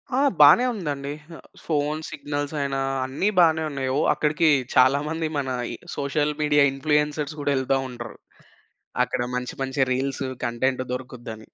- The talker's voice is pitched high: No, medium, 140 Hz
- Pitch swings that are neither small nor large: No, narrow, 2.3 semitones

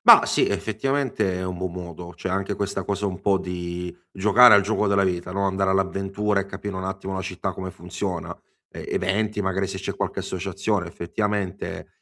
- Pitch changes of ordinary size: No, narrow, 1.7 semitones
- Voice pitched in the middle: No, very low, 95 Hz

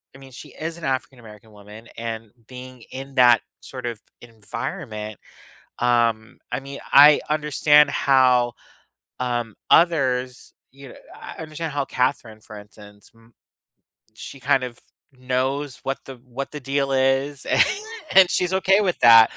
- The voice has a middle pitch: No, low, 130 Hz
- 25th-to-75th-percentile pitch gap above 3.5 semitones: No, average, 3.2 semitones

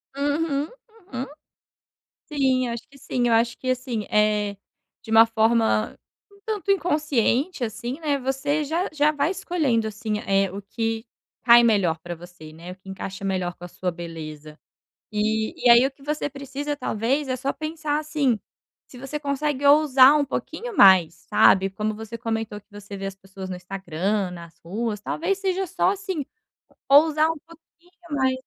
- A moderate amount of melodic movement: No, wide, 6.5 semitones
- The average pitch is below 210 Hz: No, high, 245 Hz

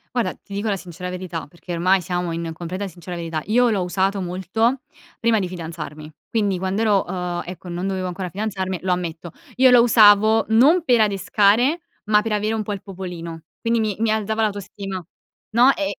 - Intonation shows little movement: No, average, 3.5 semitones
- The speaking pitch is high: Yes, high, 195 Hz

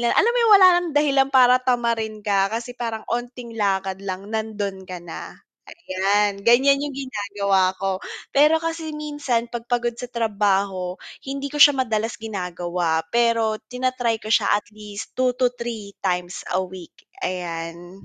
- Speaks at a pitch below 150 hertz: No, high, 220 Hz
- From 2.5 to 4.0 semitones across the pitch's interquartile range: No, average, 4.6 semitones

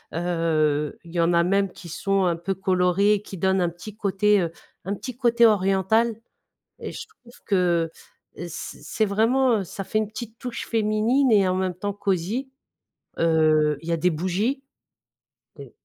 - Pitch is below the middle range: No, high, 195 Hz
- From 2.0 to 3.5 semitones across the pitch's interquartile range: No, average, 4.0 semitones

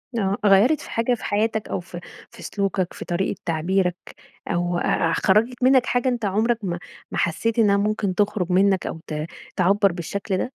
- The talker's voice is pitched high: Yes, high, 200 Hz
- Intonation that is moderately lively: Yes, average, 3.7 semitones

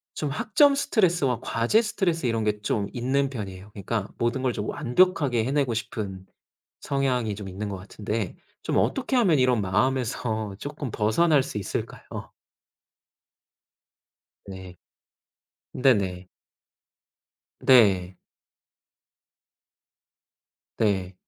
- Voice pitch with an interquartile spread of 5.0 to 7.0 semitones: Yes, average, 5.3 semitones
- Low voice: Yes, low, 115 Hz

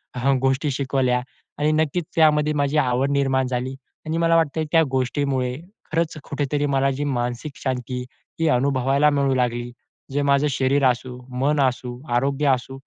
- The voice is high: No, low, 135 Hz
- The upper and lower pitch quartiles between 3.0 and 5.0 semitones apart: No, narrow, 2.4 semitones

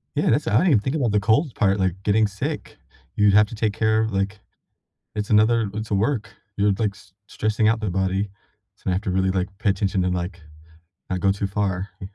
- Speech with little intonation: Yes, narrow, 2.1 semitones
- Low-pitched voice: Yes, low, 105 Hz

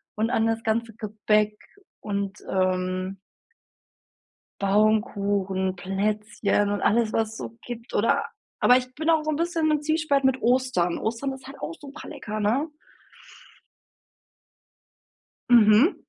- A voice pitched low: No, high, 220 Hz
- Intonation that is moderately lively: Yes, average, 4.3 semitones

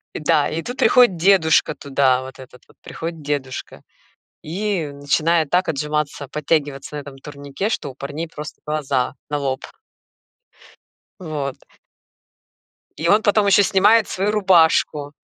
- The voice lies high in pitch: No, medium, 150 Hz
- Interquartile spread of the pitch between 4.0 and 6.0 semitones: Yes, average, 4.4 semitones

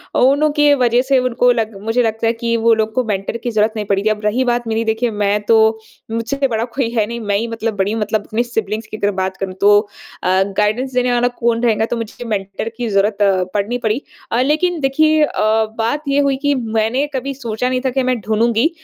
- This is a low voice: No, high, 230 Hz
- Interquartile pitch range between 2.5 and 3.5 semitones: Yes, average, 2.8 semitones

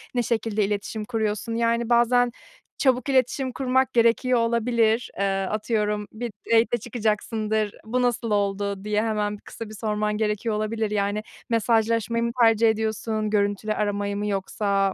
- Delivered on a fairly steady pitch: Yes, narrow, 1.9 semitones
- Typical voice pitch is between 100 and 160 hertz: No, high, 220 Hz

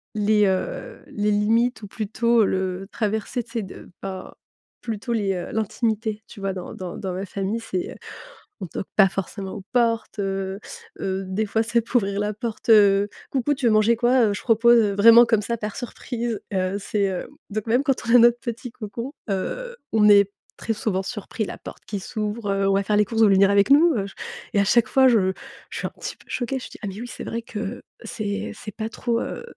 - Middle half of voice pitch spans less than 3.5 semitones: Yes, average, 2.9 semitones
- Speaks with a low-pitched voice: No, high, 215 Hz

